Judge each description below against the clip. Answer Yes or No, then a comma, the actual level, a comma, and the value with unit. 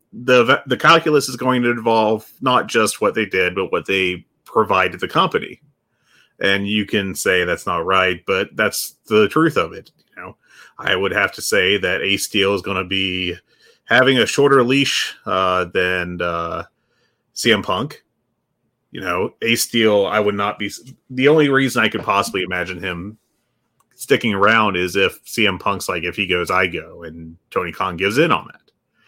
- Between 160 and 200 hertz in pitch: No, low, 105 Hz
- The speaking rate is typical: Yes, average, 185 wpm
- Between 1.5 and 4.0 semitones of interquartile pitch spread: No, average, 4.6 semitones